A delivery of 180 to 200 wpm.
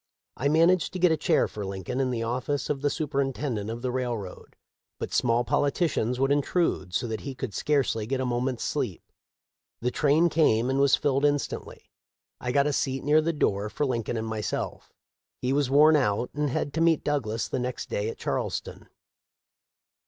Yes: average, 190 wpm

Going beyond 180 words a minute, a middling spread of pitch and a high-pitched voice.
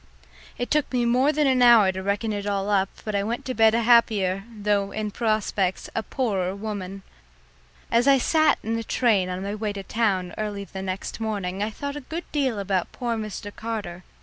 Yes: fast, 205 wpm; average, 3.1 semitones; high, 215 Hz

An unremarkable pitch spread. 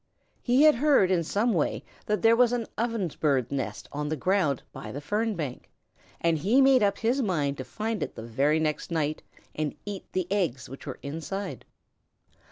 No: wide, 7.4 semitones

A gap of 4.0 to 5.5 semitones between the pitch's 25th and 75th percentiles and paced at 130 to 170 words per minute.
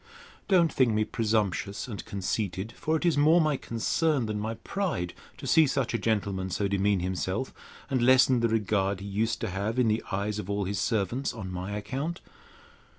No: average, 4.6 semitones; average, 190 wpm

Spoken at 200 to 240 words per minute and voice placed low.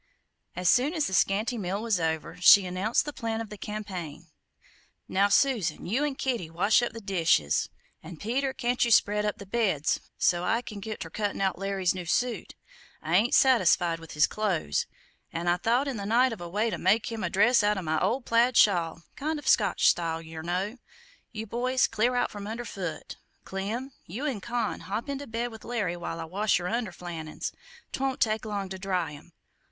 No: fast, 205 wpm; high, 205 Hz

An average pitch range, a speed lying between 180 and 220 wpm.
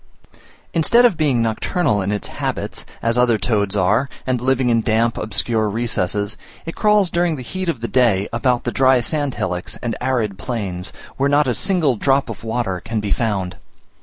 Yes: average, 4.3 semitones; average, 185 wpm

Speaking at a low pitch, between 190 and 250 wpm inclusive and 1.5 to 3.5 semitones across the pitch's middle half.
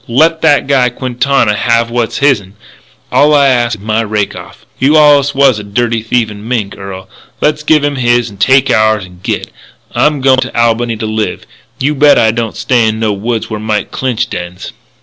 No: low, 120 Hz; average, 195 wpm; average, 3.9 semitones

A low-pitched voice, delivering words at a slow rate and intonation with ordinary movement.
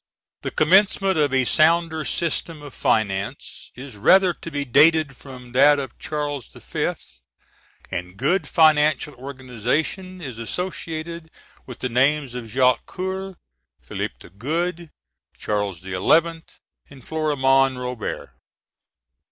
No: medium, 145 Hz; slow, 120 wpm; average, 4.5 semitones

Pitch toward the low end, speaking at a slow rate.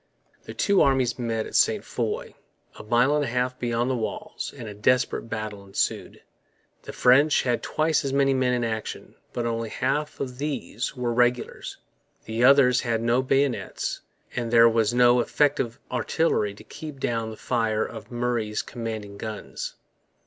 No: low, 120 Hz; average, 165 wpm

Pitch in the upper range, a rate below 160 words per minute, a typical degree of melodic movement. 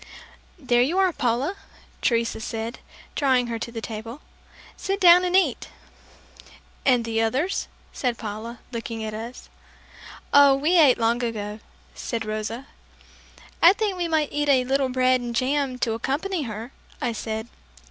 Yes: very high, 250 Hz; average, 150 wpm; average, 4.2 semitones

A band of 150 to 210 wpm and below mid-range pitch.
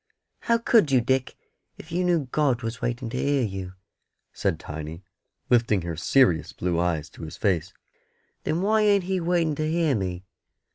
Yes: average, 175 wpm; low, 125 Hz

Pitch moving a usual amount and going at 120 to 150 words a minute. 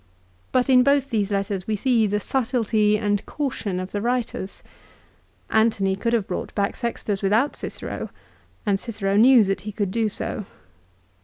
No: average, 3.1 semitones; average, 160 wpm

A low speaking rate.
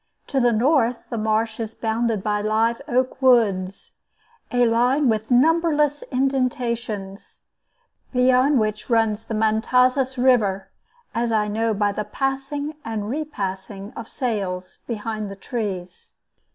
Yes: slow, 125 wpm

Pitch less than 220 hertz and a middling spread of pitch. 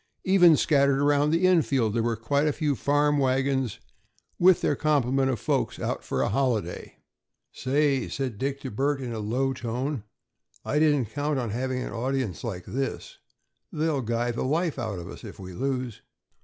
Yes: low, 135 Hz; average, 3.6 semitones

